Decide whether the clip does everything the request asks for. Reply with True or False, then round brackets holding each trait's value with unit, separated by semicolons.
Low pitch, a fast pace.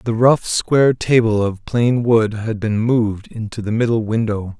False (110 Hz; 185 wpm)